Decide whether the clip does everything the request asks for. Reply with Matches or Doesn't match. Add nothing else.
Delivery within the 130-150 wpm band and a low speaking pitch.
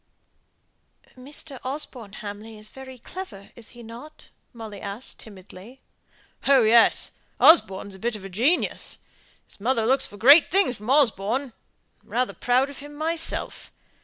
Doesn't match